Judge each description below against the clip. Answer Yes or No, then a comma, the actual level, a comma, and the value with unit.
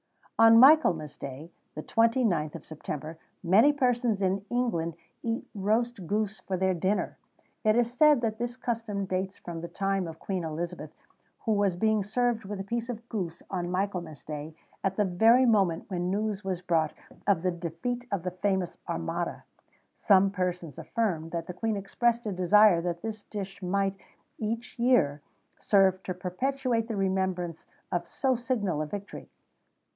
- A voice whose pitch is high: Yes, high, 195 Hz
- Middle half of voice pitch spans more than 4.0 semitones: Yes, average, 4.5 semitones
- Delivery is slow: No, average, 165 wpm